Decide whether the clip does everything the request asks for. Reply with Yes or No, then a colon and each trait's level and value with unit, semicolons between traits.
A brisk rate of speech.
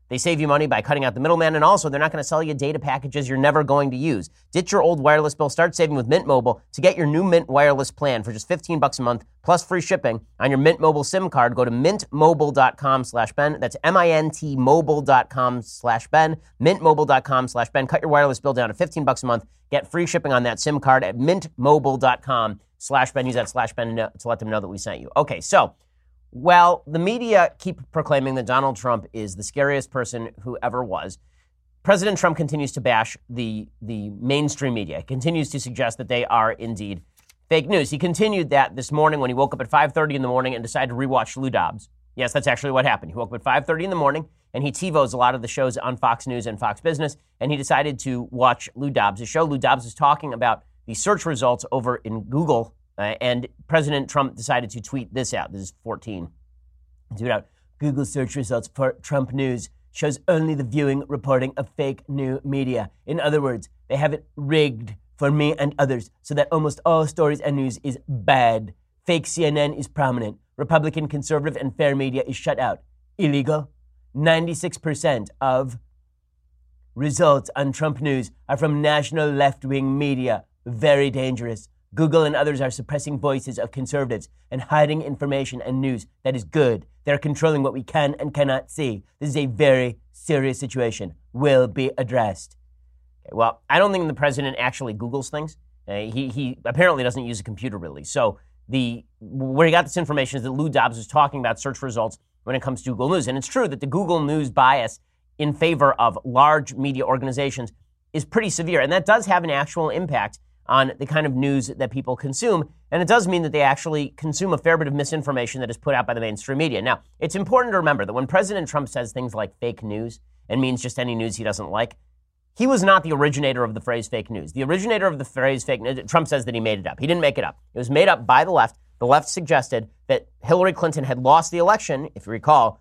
Yes: fast, 210 wpm